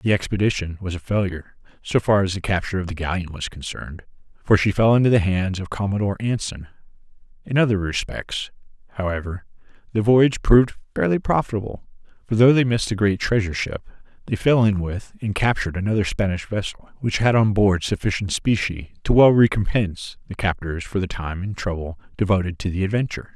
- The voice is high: No, low, 100 Hz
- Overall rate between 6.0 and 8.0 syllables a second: Yes, 6.1 syllables/s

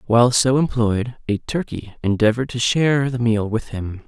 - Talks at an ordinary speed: Yes, average, 175 wpm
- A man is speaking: Yes, male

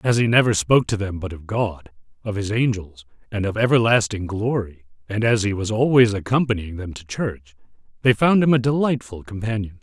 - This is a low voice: Yes, low, 110 Hz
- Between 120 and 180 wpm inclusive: No, average, 190 wpm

